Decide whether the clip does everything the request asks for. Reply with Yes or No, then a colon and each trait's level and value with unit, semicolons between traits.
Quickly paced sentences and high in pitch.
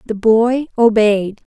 No: slow, 115 wpm; high, 220 Hz